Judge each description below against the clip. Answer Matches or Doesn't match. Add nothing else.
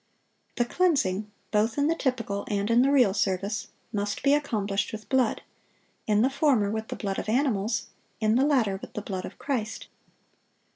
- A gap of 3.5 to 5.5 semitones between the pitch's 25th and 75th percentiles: Matches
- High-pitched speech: Matches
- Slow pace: Doesn't match